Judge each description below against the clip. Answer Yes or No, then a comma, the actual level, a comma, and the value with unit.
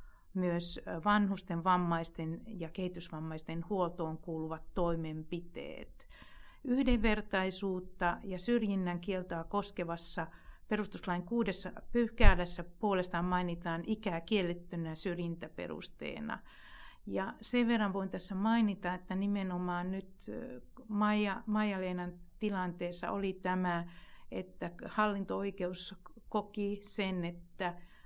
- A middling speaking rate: No, slow, 85 wpm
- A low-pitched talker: No, medium, 185 Hz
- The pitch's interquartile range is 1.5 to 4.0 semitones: Yes, average, 2.9 semitones